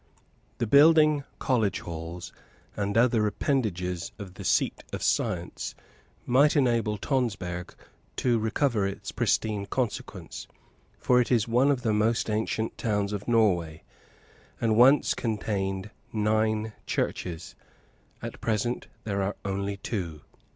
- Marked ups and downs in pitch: No, average, 3.5 semitones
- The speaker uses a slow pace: Yes, slow, 125 wpm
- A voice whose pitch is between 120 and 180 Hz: No, low, 110 Hz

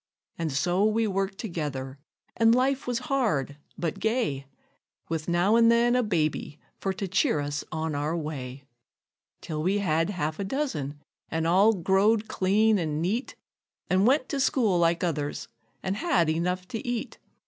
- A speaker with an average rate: Yes, average, 160 wpm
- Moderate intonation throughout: No, wide, 6.1 semitones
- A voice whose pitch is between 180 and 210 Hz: Yes, medium, 185 Hz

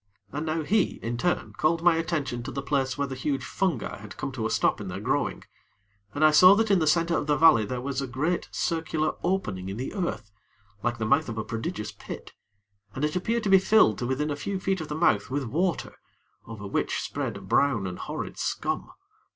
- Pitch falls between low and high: Yes, medium, 145 Hz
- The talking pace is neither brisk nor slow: No, fast, 230 wpm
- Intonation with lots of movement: Yes, wide, 5.9 semitones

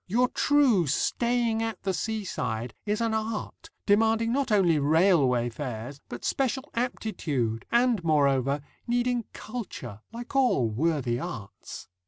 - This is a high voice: Yes, high, 205 Hz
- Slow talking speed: Yes, slow, 125 wpm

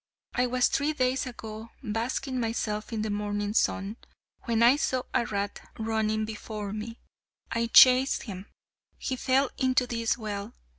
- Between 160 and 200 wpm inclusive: No, average, 150 wpm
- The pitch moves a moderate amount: Yes, average, 3.0 semitones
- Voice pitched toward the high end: Yes, high, 230 Hz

